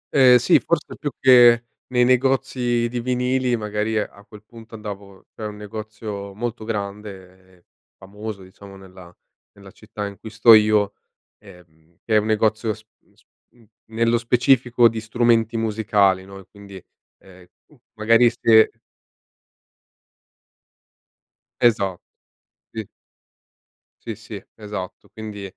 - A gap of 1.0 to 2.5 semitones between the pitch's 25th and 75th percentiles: No, average, 2.9 semitones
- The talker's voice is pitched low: Yes, low, 110 Hz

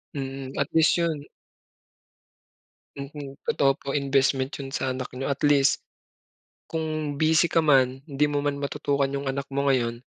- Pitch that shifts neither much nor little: No, narrow, 1.4 semitones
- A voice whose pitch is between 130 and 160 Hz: Yes, medium, 140 Hz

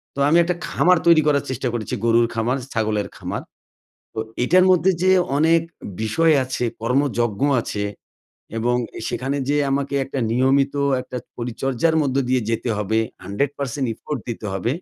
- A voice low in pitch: Yes, low, 130 Hz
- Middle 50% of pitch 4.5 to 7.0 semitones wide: No, average, 4.0 semitones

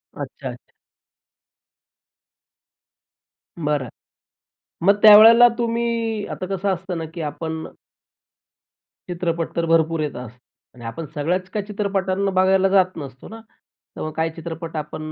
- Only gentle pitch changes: No, average, 3.8 semitones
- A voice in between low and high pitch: Yes, medium, 175 Hz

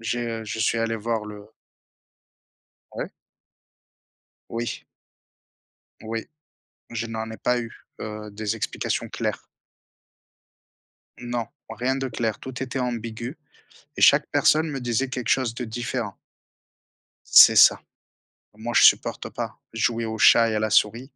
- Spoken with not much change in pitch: Yes, narrow, 1.7 semitones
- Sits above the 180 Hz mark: No, low, 115 Hz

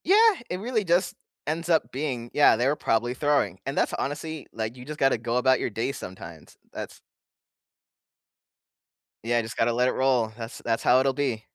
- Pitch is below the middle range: Yes, low, 130 Hz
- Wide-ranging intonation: No, average, 4.3 semitones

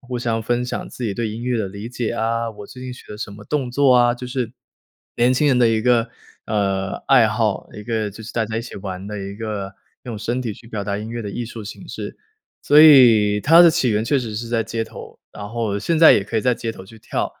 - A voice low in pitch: Yes, low, 115 Hz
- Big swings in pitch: No, average, 2.7 semitones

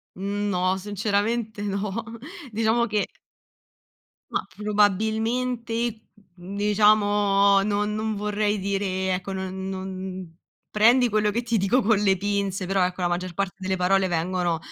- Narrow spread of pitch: Yes, narrow, 2.1 semitones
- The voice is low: No, high, 205 Hz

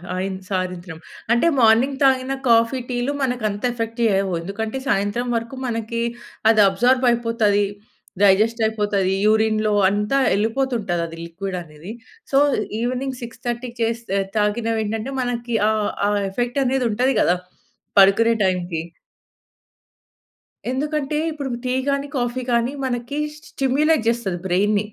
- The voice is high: Yes, high, 230 Hz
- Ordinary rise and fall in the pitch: Yes, average, 3.7 semitones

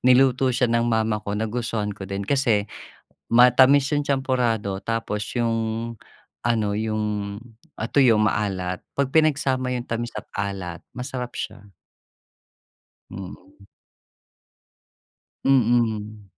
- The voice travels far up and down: No, average, 3.5 semitones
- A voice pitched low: Yes, low, 115 Hz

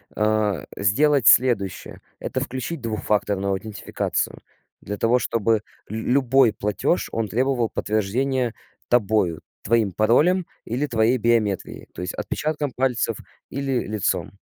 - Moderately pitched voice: No, low, 115 Hz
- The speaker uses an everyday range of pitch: Yes, average, 3.7 semitones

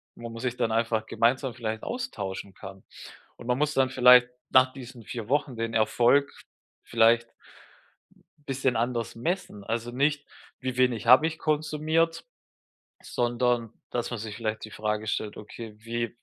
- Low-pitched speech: Yes, low, 120 Hz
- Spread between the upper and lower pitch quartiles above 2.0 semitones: Yes, narrow, 2.5 semitones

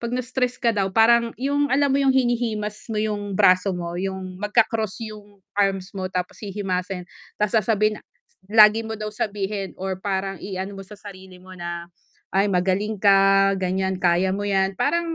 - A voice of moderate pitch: No, high, 200 Hz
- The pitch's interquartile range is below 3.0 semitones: Yes, narrow, 2.4 semitones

